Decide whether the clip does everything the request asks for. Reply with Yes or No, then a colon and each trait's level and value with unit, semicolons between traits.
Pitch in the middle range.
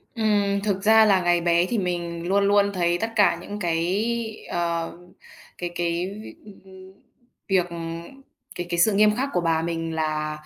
Yes: medium, 180 Hz